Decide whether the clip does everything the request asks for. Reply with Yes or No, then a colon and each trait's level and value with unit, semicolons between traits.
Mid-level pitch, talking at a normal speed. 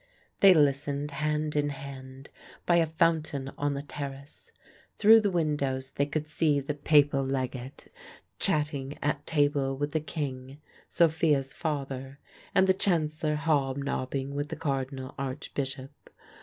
No: medium, 145 Hz; slow, 130 wpm